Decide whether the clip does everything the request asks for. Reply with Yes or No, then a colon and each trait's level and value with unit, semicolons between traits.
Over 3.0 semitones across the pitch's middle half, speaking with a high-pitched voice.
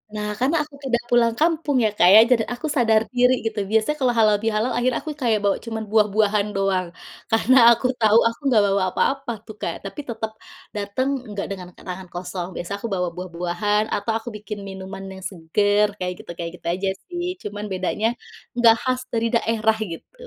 Yes: average, 3.5 semitones; high, 215 Hz